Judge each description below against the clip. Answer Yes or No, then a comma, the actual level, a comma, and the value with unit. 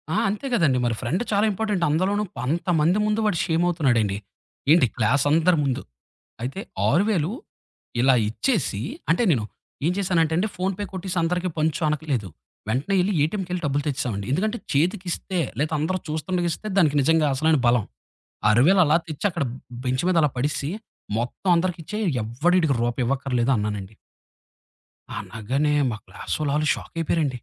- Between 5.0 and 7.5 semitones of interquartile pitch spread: Yes, wide, 5.5 semitones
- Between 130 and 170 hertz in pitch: Yes, medium, 155 Hz